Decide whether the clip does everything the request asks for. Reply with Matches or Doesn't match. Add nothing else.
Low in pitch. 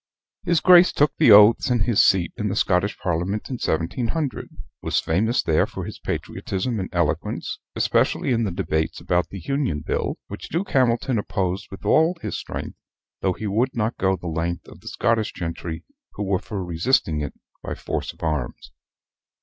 Matches